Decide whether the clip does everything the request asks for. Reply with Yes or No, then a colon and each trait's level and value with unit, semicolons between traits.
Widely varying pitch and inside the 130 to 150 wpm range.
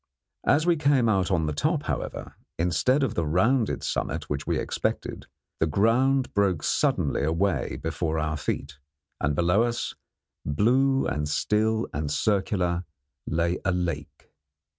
Yes: wide, 6.5 semitones; average, 140 wpm